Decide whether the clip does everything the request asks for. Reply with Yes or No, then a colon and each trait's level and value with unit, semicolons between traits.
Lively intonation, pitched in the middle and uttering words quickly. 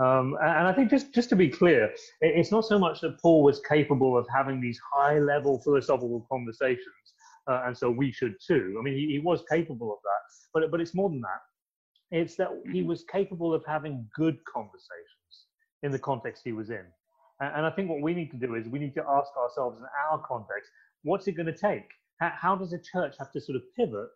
Yes: wide, 5.9 semitones; medium, 160 Hz; fast, 230 wpm